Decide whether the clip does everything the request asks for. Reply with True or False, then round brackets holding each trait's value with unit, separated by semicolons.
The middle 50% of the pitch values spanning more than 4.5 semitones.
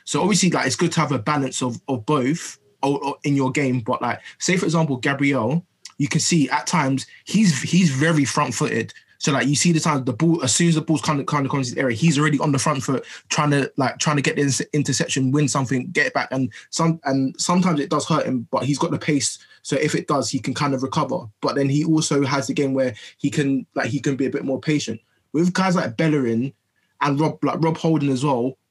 False (2.7 semitones)